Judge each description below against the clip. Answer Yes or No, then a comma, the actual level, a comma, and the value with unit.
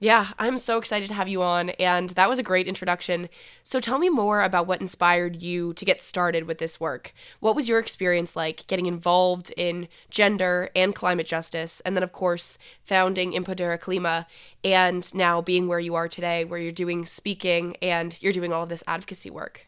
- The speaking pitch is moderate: Yes, medium, 180 Hz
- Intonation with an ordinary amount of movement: No, narrow, 1.6 semitones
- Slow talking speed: No, average, 200 wpm